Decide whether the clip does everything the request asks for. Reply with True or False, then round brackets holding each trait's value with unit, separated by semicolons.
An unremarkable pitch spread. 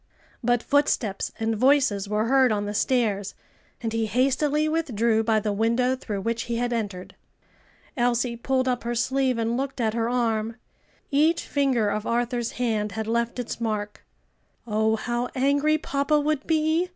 True (3.3 semitones)